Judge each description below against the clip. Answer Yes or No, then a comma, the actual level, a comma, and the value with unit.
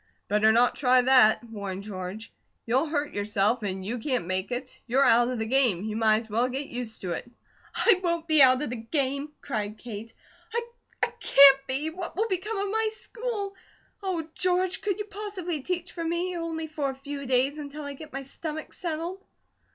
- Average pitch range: No, wide, 6.8 semitones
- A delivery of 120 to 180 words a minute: No, average, 195 wpm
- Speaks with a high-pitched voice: Yes, very high, 275 Hz